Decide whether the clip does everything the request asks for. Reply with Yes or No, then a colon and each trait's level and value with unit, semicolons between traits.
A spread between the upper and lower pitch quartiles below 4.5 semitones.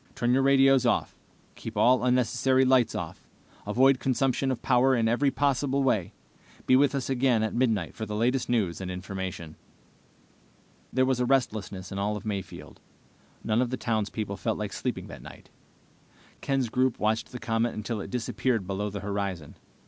Yes: average, 3.9 semitones